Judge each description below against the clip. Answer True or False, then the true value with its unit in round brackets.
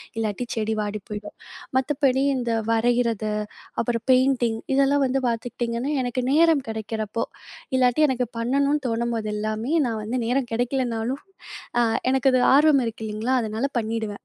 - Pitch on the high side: True (240 Hz)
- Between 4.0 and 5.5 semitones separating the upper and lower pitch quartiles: False (2.9 semitones)